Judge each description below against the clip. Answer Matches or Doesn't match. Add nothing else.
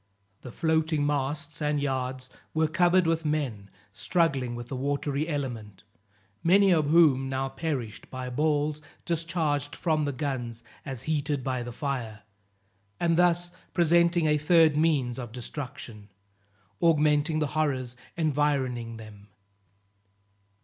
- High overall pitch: Doesn't match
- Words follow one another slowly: Matches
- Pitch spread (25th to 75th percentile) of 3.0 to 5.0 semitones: Matches